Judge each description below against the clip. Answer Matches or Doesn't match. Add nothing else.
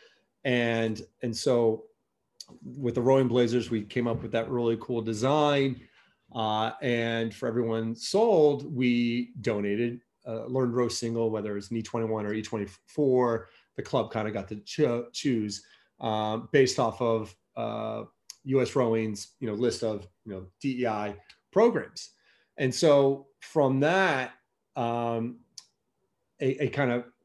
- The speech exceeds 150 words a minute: Doesn't match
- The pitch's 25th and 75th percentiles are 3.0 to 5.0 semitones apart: Doesn't match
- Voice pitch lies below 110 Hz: Doesn't match